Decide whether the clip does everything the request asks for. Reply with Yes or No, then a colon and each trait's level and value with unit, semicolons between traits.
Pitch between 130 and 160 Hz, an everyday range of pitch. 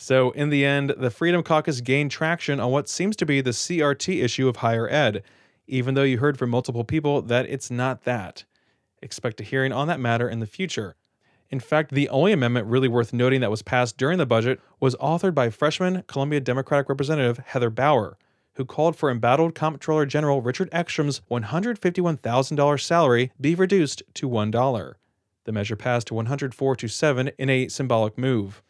Yes: low, 135 Hz; average, 3.6 semitones